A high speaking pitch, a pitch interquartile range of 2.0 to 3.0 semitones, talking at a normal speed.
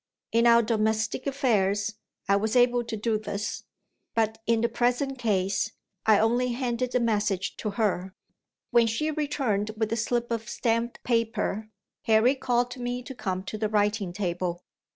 Yes: high, 225 Hz; average, 2.7 semitones; average, 165 wpm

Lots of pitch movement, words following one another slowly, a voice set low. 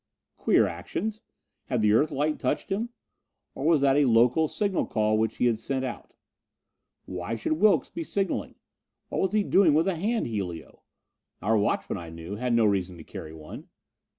No: wide, 7.8 semitones; average, 180 wpm; low, 125 Hz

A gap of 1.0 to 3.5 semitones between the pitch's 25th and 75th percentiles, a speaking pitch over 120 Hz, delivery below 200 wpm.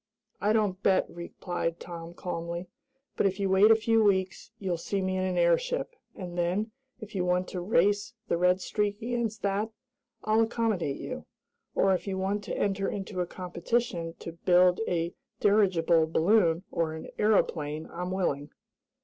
Yes: average, 3.2 semitones; medium, 185 Hz; average, 165 wpm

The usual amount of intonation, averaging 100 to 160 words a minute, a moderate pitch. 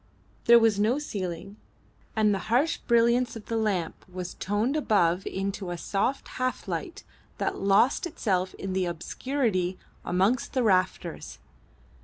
No: average, 4.3 semitones; average, 140 wpm; high, 205 Hz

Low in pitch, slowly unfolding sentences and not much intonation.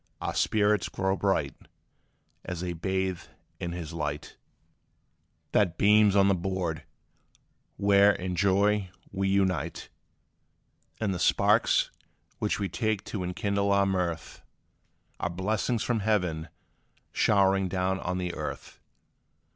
Yes: very low, 95 Hz; slow, 120 wpm; narrow, 2.2 semitones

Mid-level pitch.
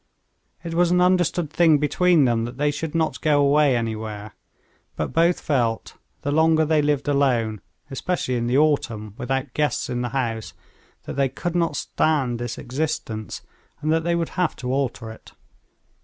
Yes: medium, 145 Hz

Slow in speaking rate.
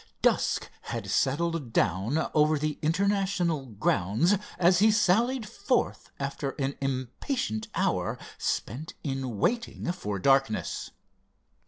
Yes: slow, 110 wpm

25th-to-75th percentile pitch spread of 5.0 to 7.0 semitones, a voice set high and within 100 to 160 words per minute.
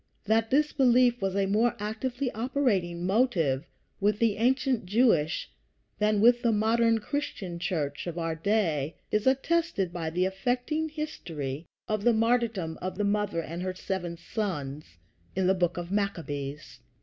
Yes: wide, 5.5 semitones; high, 205 Hz; average, 150 wpm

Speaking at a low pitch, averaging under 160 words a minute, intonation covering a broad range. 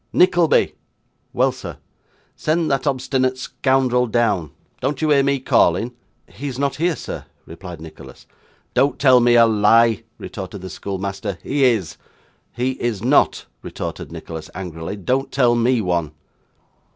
Yes: low, 120 Hz; average, 140 wpm; wide, 5.7 semitones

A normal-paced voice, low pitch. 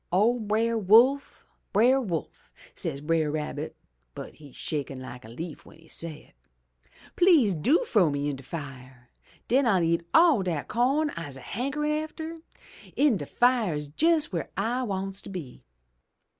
No: average, 155 wpm; high, 190 Hz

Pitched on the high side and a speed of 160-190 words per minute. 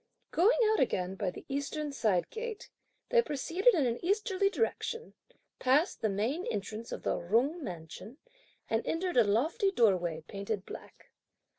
No: very high, 260 Hz; average, 150 wpm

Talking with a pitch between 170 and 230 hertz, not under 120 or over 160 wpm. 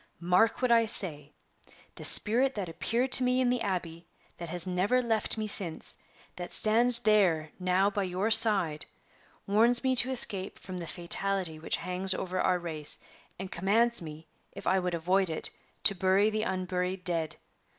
No: high, 190 Hz; average, 170 wpm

